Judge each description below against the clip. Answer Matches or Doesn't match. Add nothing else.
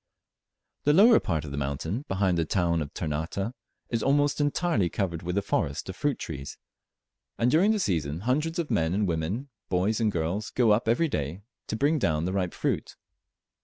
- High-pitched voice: Doesn't match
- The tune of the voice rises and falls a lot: Matches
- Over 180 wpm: Matches